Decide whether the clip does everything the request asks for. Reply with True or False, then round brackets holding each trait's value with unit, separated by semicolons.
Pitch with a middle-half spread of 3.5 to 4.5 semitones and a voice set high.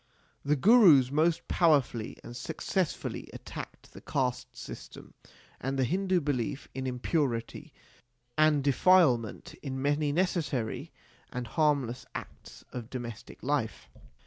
False (4.0 semitones; 140 Hz)